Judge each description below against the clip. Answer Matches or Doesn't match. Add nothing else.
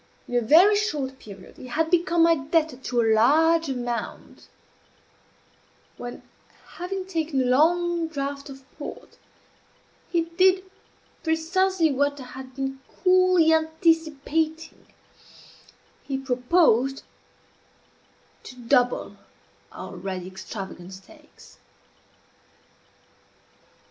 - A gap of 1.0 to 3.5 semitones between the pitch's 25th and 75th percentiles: Doesn't match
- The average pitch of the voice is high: Matches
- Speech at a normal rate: Doesn't match